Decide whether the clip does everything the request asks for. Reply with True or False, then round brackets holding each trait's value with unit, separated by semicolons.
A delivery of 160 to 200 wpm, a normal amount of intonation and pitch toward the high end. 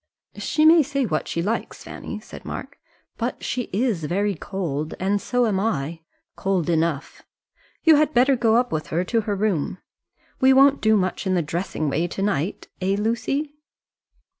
False (175 wpm; 6.4 semitones; 200 Hz)